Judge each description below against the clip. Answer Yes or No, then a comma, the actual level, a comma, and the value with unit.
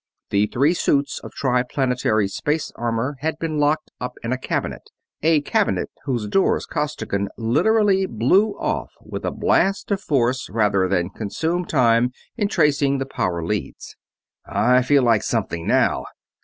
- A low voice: Yes, low, 130 Hz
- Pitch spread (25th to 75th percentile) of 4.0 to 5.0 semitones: No, wide, 5.6 semitones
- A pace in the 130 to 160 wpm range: Yes, average, 150 wpm